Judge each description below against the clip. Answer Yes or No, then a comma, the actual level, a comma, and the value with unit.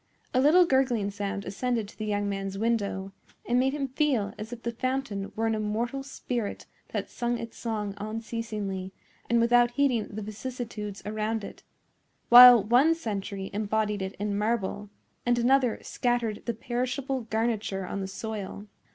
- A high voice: Yes, high, 225 Hz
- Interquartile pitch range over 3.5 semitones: No, average, 3.0 semitones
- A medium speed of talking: Yes, average, 160 wpm